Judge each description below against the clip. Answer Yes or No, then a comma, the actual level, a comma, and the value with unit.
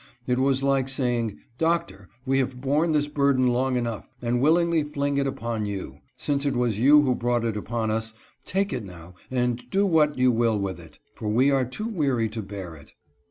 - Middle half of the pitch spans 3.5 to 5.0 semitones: Yes, average, 3.9 semitones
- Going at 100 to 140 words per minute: No, fast, 205 wpm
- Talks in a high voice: No, low, 125 Hz